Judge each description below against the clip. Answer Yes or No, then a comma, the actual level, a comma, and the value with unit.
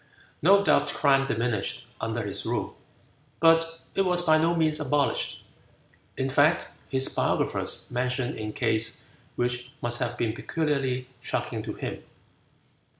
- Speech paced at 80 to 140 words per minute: Yes, slow, 135 wpm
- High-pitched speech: No, low, 130 Hz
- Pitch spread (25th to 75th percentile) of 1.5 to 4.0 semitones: No, average, 4.7 semitones